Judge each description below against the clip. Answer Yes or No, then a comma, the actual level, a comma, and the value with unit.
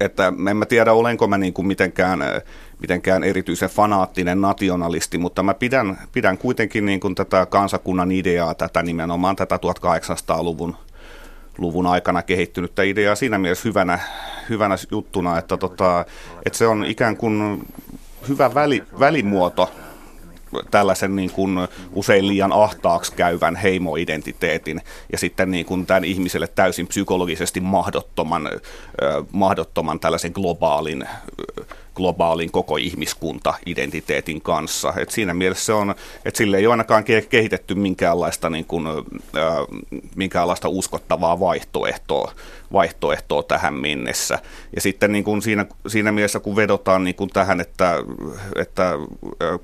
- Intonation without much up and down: Yes, narrow, 2.3 semitones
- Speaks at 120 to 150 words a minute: Yes, average, 130 wpm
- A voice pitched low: Yes, very low, 95 Hz